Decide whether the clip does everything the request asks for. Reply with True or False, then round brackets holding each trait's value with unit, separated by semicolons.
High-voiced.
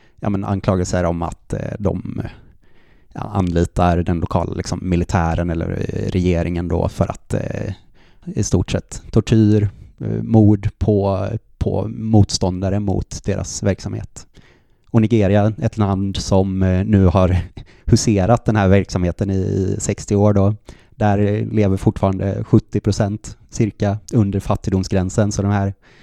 False (100 Hz)